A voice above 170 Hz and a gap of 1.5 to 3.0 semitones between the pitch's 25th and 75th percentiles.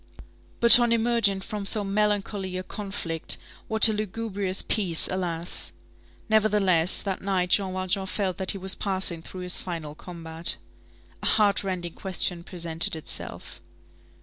Yes: high, 190 Hz; average, 2.7 semitones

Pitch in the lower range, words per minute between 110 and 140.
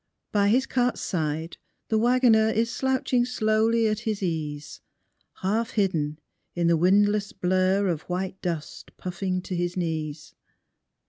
No: high, 190 Hz; slow, 135 wpm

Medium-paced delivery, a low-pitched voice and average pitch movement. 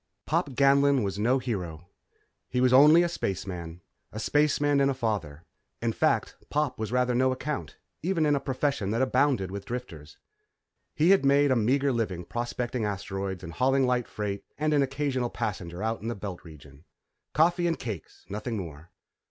No: average, 175 wpm; low, 120 Hz; wide, 6.1 semitones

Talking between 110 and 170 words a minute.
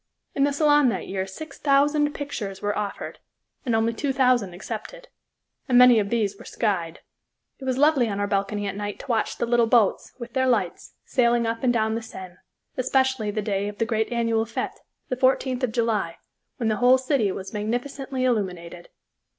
No: average, 190 wpm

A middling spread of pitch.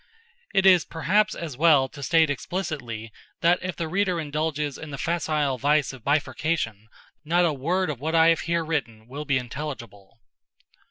Yes: average, 3.9 semitones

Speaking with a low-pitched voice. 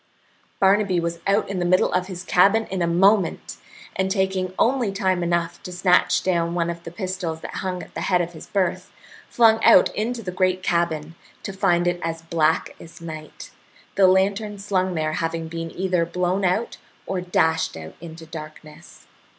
No: medium, 180 Hz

